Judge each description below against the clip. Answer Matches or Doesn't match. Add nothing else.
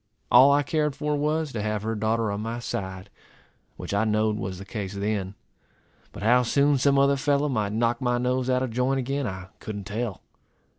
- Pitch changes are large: Doesn't match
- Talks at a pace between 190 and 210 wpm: Matches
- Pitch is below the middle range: Matches